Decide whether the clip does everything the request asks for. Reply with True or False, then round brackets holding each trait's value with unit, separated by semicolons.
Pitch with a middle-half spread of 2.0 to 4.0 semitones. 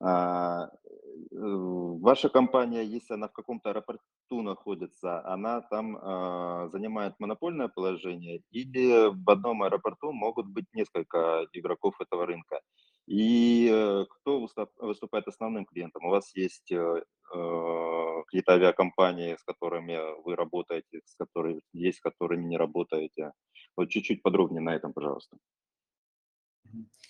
False (4.4 semitones)